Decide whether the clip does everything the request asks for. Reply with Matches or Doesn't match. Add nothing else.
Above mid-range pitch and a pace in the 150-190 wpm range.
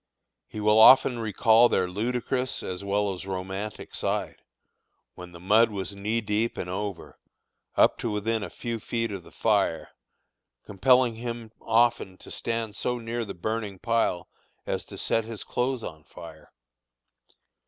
Doesn't match